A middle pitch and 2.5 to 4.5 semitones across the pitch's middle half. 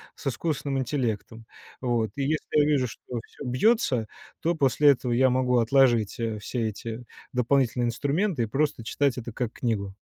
No: low, 125 Hz; average, 3.4 semitones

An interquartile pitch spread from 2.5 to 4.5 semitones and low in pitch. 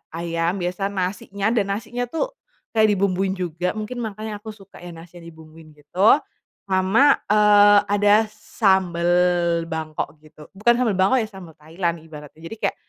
No: average, 4.0 semitones; high, 195 Hz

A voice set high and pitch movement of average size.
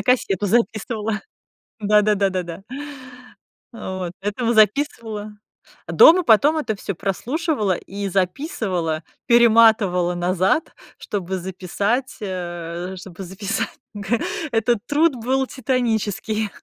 Yes: high, 210 Hz; average, 4.0 semitones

